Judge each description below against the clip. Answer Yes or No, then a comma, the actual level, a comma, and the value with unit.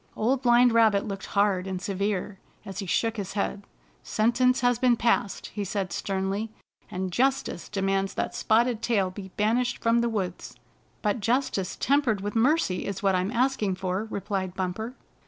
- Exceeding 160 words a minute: Yes, average, 175 wpm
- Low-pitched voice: No, high, 210 Hz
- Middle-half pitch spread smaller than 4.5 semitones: Yes, average, 3.5 semitones